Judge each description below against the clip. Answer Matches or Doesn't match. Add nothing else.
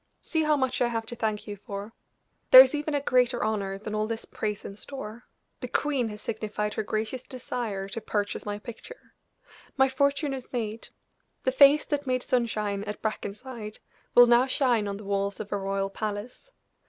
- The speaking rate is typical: Matches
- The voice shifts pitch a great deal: Doesn't match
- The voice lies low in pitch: Doesn't match